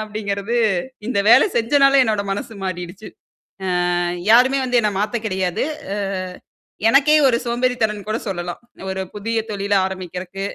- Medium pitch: No, high, 215 Hz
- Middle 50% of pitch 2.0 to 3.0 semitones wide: No, average, 3.8 semitones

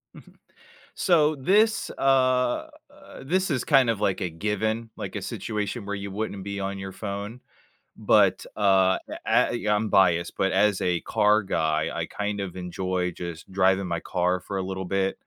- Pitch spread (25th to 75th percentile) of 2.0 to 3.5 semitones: Yes, average, 2.8 semitones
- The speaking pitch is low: Yes, low, 100 Hz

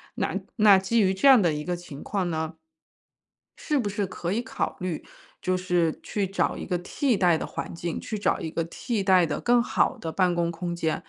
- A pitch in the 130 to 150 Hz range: No, medium, 185 Hz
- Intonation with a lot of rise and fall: No, average, 3.3 semitones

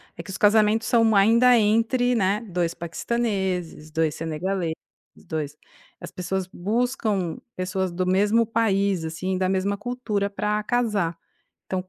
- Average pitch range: Yes, average, 3.6 semitones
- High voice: Yes, high, 195 Hz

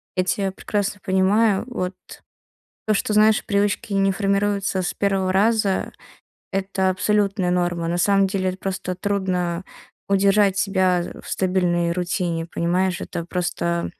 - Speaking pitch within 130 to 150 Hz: No, high, 190 Hz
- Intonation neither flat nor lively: No, narrow, 1.9 semitones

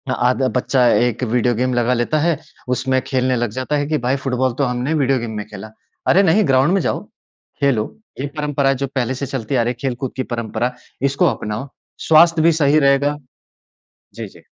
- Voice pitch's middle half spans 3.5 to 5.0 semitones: No, narrow, 2.5 semitones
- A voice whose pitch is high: No, low, 130 Hz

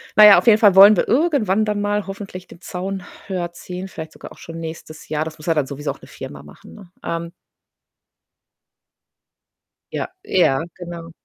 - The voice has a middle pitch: Yes, medium, 180 Hz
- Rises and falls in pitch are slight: No, average, 4.0 semitones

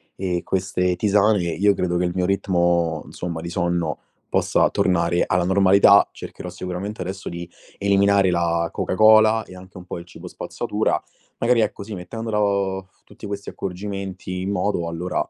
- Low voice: Yes, very low, 95 Hz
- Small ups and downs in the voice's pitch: Yes, narrow, 2.3 semitones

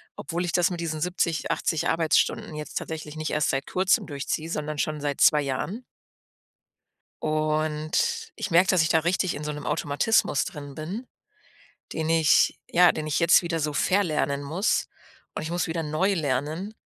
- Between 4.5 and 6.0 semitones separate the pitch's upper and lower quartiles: No, narrow, 2.5 semitones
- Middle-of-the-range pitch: Yes, medium, 155 Hz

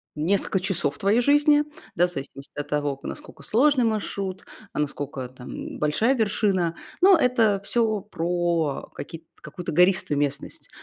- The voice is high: No, medium, 180 Hz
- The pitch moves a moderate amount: No, wide, 6.8 semitones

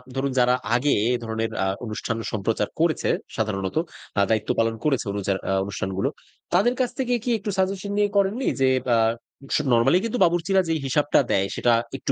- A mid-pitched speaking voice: No, low, 130 Hz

